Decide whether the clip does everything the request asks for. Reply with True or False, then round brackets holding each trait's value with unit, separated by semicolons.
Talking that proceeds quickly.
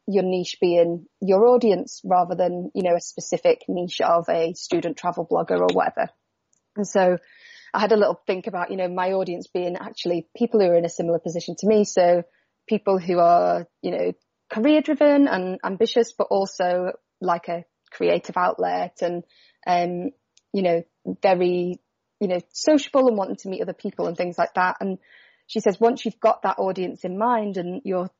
False (185 wpm)